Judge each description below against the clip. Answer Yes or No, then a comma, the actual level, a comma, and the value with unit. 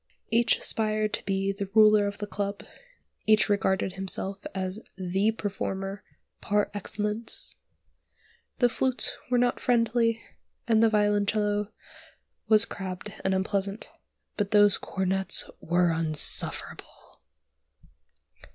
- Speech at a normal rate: No, slow, 110 wpm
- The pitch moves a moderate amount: No, narrow, 2.0 semitones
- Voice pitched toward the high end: Yes, high, 205 Hz